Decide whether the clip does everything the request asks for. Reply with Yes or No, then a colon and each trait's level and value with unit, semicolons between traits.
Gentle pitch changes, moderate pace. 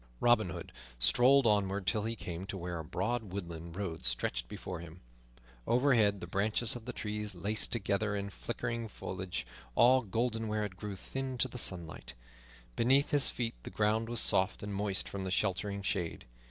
No: average, 3.7 semitones; average, 180 wpm